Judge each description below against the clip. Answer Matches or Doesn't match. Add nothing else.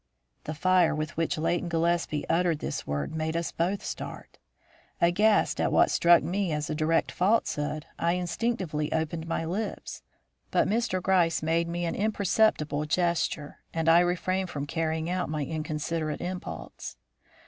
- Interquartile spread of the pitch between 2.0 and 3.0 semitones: Matches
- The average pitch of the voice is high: Doesn't match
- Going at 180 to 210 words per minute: Doesn't match